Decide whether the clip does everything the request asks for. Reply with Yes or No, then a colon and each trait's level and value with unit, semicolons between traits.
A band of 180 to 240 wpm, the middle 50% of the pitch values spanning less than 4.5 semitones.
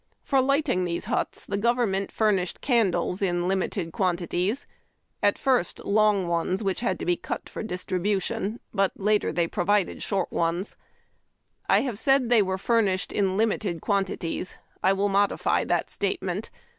No: average, 155 wpm; average, 2.9 semitones